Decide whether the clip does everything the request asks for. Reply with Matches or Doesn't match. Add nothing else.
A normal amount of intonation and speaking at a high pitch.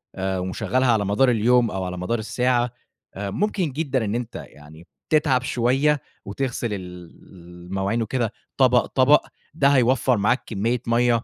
Doesn't match